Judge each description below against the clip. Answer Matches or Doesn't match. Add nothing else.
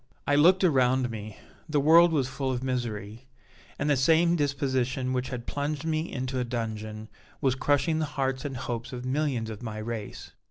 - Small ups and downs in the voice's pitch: Doesn't match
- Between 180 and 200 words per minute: Matches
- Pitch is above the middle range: Doesn't match